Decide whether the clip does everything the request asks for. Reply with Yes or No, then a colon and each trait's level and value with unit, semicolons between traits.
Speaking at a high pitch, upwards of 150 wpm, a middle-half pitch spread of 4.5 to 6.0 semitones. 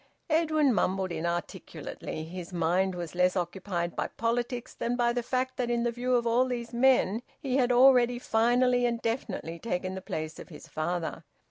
Yes: high, 230 Hz; average, 175 wpm; wide, 5.6 semitones